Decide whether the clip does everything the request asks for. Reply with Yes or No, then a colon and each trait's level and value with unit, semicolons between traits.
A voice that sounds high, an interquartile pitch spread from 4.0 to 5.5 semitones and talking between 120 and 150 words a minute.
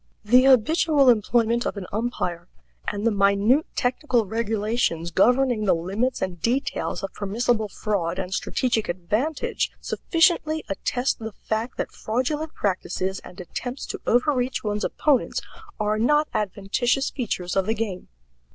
Yes: high, 225 Hz; average, 4.3 semitones; slow, 135 wpm